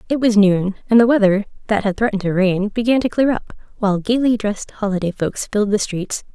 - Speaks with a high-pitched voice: Yes, high, 210 Hz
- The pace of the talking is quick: Yes, fast, 210 wpm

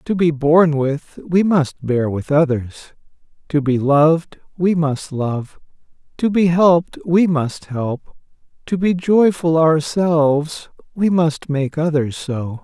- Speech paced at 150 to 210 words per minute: No, average, 140 wpm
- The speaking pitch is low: No, medium, 155 Hz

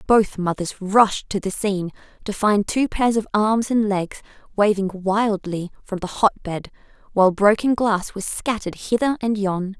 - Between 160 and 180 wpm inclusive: Yes, average, 170 wpm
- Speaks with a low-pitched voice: No, high, 205 Hz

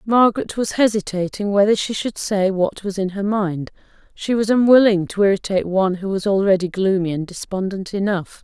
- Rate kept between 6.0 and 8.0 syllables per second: No, 5.4 syllables/s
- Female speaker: Yes, female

